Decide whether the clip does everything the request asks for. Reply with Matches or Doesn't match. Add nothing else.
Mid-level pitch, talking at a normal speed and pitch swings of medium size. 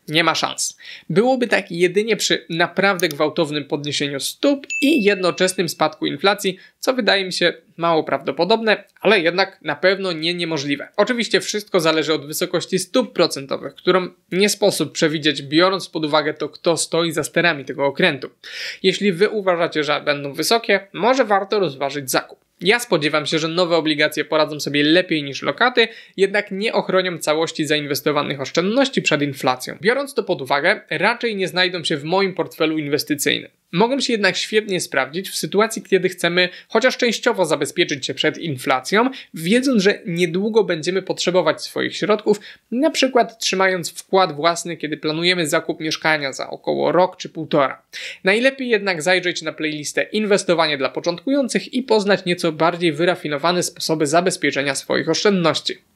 Matches